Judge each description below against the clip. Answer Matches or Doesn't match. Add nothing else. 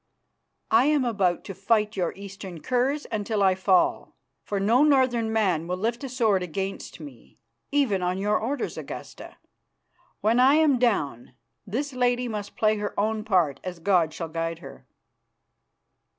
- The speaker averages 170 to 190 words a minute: Doesn't match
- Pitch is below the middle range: Doesn't match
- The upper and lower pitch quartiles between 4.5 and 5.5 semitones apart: Matches